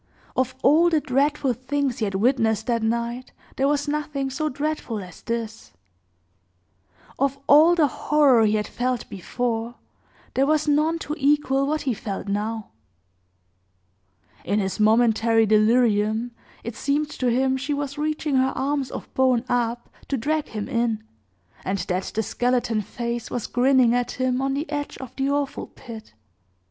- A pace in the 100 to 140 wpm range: No, average, 155 wpm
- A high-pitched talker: Yes, very high, 255 Hz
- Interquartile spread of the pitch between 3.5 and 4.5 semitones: Yes, average, 4.0 semitones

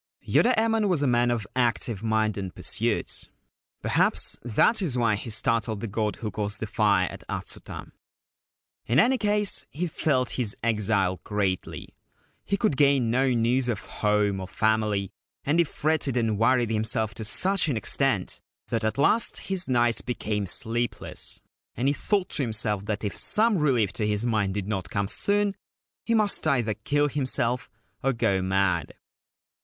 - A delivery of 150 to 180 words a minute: Yes, average, 165 wpm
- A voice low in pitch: Yes, low, 115 Hz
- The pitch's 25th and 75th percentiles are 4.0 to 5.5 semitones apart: Yes, average, 5.2 semitones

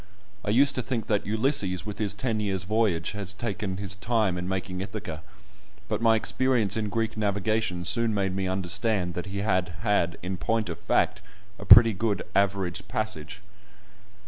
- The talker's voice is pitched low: Yes, low, 100 Hz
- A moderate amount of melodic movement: Yes, average, 3.0 semitones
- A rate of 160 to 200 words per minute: Yes, average, 170 wpm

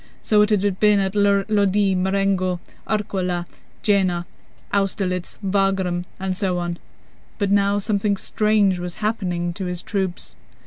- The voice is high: Yes, high, 195 Hz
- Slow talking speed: Yes, slow, 130 wpm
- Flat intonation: Yes, narrow, 2.0 semitones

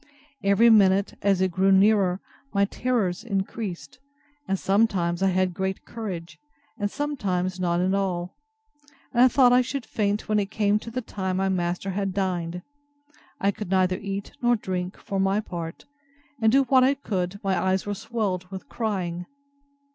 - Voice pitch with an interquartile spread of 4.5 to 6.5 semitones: No, average, 2.7 semitones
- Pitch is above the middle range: Yes, high, 195 Hz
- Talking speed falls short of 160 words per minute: No, average, 170 wpm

